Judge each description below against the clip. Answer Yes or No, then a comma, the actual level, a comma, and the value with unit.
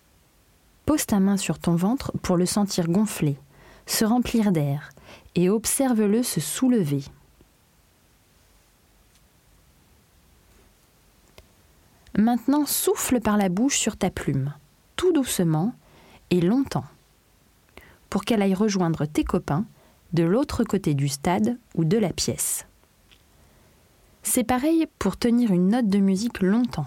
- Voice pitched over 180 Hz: Yes, high, 190 Hz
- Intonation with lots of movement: Yes, wide, 8.6 semitones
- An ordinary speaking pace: No, slow, 120 wpm